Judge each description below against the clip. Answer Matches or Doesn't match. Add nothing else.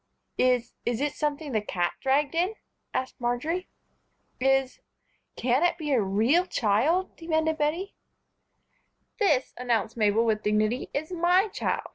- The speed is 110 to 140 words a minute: Matches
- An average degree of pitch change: Doesn't match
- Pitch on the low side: Doesn't match